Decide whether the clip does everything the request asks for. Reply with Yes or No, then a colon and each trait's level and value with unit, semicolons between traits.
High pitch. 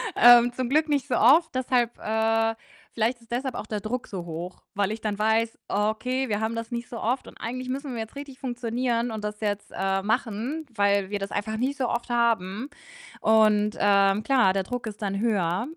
Yes: high, 225 Hz